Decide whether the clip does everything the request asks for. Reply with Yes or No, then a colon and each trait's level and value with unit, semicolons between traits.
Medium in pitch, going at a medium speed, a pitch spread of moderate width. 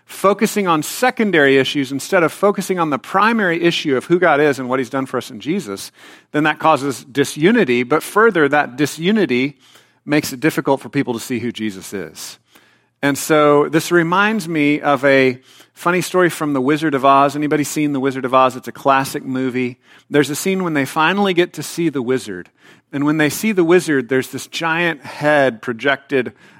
Yes: medium, 145 Hz; average, 195 wpm; average, 3.8 semitones